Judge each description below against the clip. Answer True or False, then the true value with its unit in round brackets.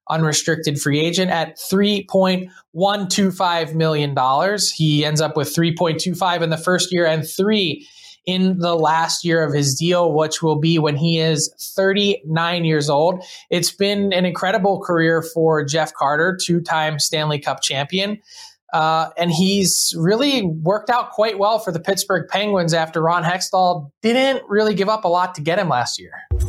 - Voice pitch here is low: False (175 Hz)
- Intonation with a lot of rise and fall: False (3.3 semitones)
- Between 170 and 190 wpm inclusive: True (180 wpm)